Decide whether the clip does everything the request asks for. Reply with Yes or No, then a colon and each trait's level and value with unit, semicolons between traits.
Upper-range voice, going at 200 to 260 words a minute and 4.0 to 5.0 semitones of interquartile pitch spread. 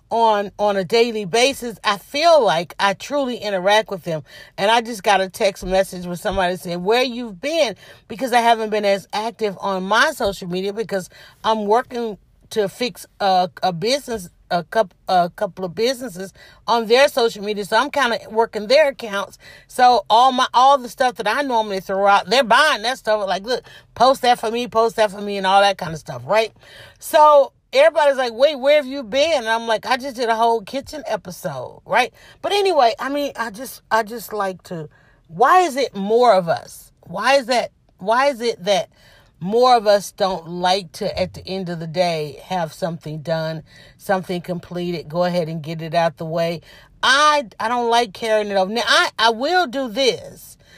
Yes: high, 215 Hz; fast, 205 wpm; average, 4.7 semitones